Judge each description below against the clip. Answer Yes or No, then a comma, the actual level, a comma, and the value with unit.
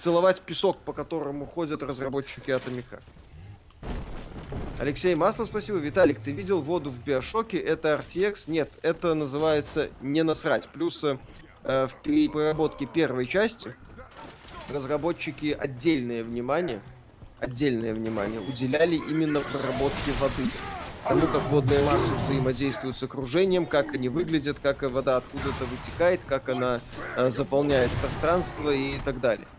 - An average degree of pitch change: Yes, average, 3.6 semitones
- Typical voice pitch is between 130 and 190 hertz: Yes, medium, 140 Hz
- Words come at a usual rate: Yes, average, 120 wpm